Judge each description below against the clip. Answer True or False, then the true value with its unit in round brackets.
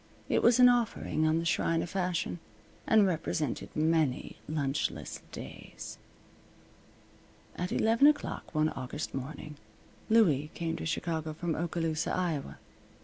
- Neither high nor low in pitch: True (165 Hz)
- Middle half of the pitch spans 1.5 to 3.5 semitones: True (3.1 semitones)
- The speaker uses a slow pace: True (125 wpm)